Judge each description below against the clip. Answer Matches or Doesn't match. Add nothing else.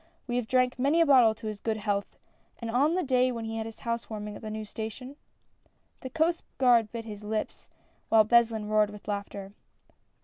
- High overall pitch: Matches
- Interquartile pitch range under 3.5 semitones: Matches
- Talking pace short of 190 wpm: Doesn't match